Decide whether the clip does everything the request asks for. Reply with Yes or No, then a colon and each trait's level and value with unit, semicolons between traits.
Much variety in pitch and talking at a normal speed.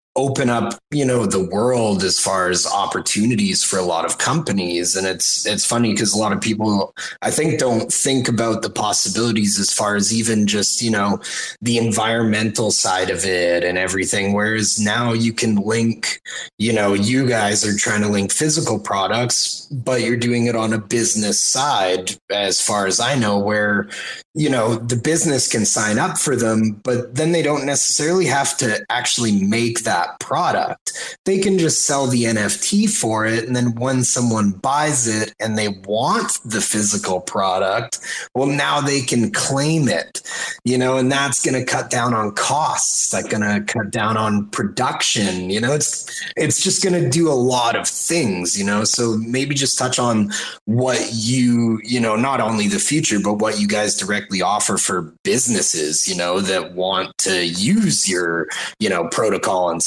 No: average, 3.9 semitones; average, 185 wpm